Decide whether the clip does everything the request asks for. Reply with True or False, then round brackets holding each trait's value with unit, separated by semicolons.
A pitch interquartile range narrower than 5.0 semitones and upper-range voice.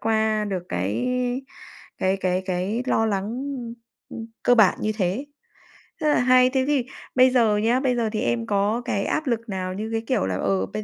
True (4.6 semitones; 215 Hz)